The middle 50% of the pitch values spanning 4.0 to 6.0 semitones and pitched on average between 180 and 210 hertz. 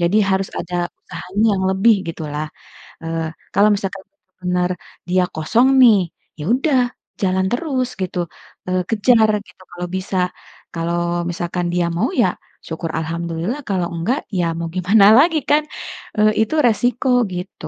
Yes: average, 4.4 semitones; medium, 185 Hz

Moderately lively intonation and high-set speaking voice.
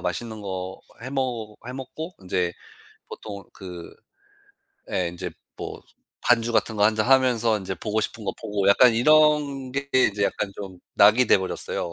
No: average, 4.9 semitones; low, 110 Hz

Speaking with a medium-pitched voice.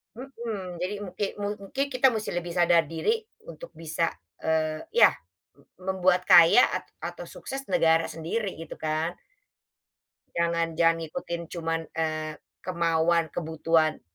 Yes: medium, 170 Hz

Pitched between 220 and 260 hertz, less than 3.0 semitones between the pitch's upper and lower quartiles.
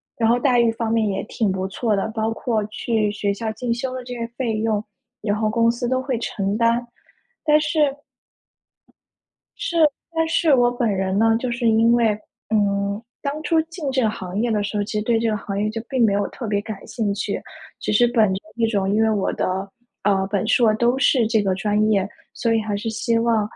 Yes: high, 225 Hz; narrow, 2.6 semitones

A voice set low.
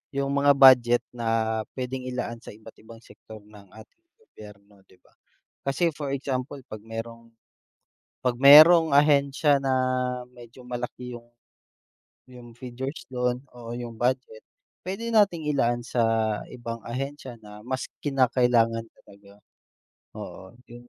Yes: low, 125 Hz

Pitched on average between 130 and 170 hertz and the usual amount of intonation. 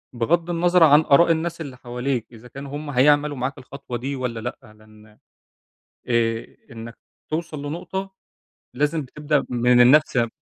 Yes: medium, 140 Hz; average, 4.1 semitones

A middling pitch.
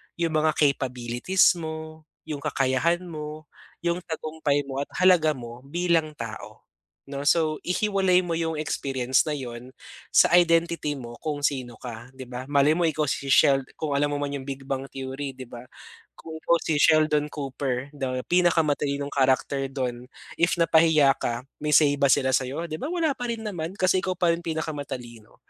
Yes: medium, 150 Hz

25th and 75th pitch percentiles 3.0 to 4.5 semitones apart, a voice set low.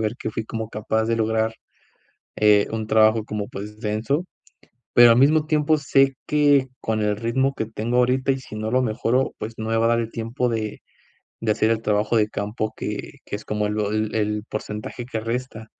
No: narrow, 2.5 semitones; low, 110 Hz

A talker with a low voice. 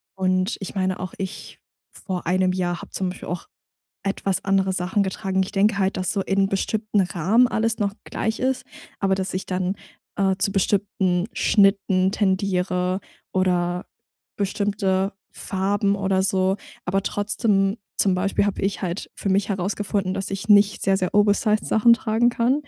No: high, 195 Hz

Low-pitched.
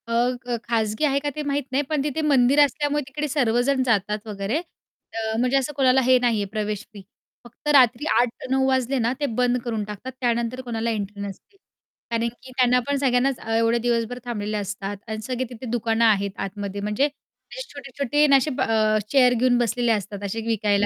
No: high, 240 Hz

